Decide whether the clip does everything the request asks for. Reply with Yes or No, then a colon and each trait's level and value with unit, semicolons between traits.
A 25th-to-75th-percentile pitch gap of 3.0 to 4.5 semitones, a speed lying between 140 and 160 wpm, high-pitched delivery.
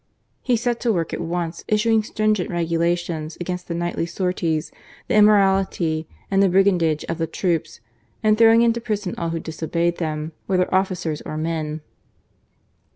No: average, 3.6 semitones; average, 155 wpm; medium, 175 Hz